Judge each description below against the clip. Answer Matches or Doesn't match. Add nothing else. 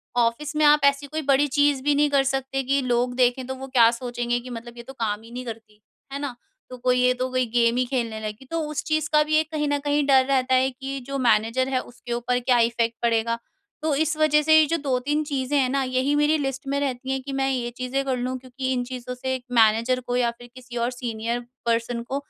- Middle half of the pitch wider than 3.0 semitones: Doesn't match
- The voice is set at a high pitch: Matches